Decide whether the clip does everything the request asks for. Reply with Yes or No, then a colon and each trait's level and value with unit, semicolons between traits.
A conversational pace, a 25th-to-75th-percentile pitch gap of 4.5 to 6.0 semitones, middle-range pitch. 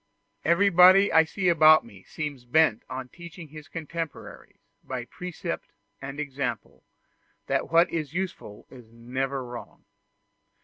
No: slow, 125 wpm; average, 4.9 semitones; medium, 150 Hz